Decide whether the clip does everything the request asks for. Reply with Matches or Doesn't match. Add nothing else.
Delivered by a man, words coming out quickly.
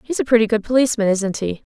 Doesn't match